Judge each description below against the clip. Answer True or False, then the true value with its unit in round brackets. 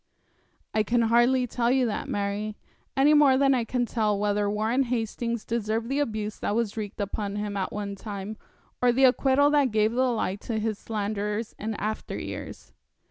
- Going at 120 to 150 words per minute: False (185 wpm)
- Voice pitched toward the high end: True (220 Hz)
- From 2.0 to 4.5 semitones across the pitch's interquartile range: True (3.0 semitones)